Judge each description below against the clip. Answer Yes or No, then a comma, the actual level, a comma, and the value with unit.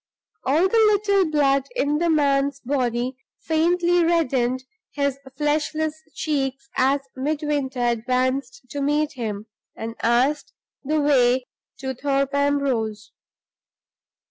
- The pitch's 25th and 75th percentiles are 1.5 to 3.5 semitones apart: Yes, average, 3.0 semitones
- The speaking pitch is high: Yes, very high, 280 Hz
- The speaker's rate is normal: No, slow, 110 wpm